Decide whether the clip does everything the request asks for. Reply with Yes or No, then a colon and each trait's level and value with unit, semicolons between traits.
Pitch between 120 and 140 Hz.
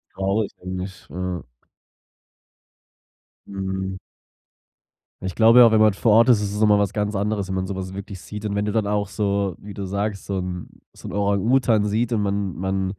No: low, 100 Hz